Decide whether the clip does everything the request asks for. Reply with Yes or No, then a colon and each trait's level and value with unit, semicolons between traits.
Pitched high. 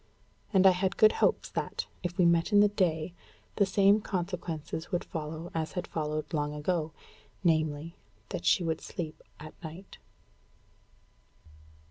No: medium, 170 Hz